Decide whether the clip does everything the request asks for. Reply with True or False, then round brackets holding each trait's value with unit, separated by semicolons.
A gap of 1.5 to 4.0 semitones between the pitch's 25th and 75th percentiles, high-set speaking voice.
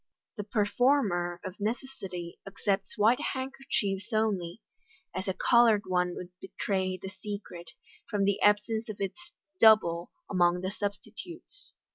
True (3.1 semitones; 205 Hz)